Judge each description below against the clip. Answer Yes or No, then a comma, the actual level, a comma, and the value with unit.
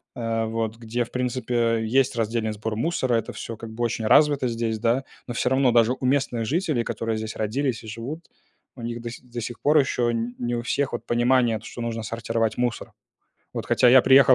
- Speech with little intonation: Yes, narrow, 1.9 semitones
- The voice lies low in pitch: Yes, low, 120 Hz